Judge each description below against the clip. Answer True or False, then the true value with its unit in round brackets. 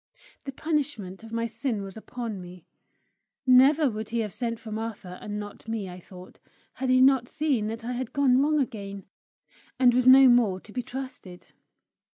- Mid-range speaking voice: False (230 Hz)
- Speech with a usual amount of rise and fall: True (3.9 semitones)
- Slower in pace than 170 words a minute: False (180 wpm)